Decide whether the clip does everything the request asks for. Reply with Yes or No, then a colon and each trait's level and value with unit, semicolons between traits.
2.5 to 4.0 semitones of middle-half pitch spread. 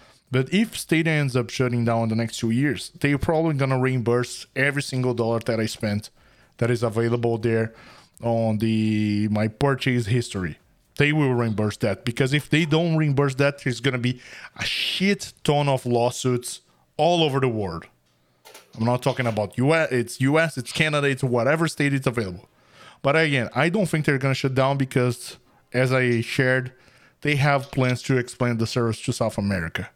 Yes: average, 3.4 semitones